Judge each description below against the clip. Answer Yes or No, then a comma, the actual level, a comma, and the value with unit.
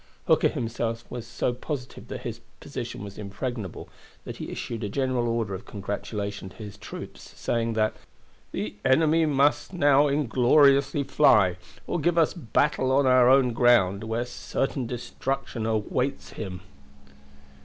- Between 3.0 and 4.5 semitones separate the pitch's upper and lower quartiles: Yes, average, 3.8 semitones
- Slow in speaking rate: No, average, 145 wpm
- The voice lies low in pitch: Yes, low, 120 Hz